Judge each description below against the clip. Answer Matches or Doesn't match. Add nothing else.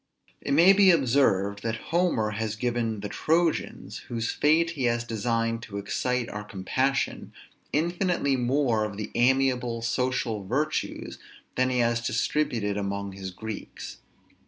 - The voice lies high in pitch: Doesn't match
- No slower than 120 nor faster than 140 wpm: Matches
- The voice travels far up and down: Doesn't match